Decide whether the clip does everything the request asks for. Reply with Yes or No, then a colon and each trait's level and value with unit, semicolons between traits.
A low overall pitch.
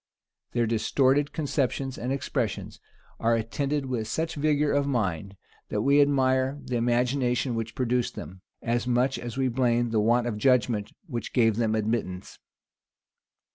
Yes: low, 125 Hz